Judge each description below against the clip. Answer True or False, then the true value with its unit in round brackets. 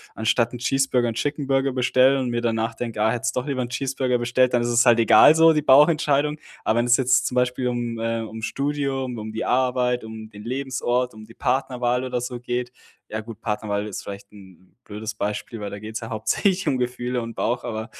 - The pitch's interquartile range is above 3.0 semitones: False (2.6 semitones)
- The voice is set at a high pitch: False (120 Hz)